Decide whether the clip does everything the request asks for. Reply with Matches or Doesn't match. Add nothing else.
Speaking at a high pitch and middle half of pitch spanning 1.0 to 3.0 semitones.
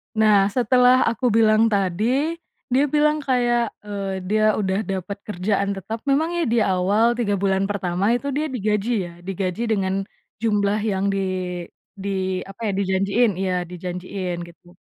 Doesn't match